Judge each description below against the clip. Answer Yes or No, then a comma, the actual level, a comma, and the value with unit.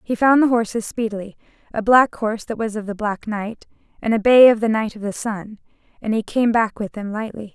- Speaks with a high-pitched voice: Yes, high, 220 Hz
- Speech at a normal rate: No, fast, 240 wpm